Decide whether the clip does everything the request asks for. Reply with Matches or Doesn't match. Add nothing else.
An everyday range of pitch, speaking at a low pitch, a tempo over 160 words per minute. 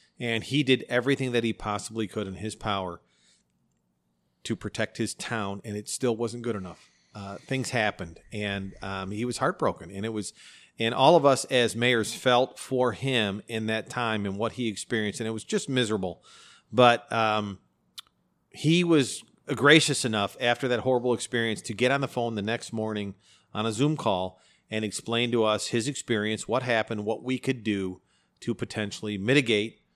Matches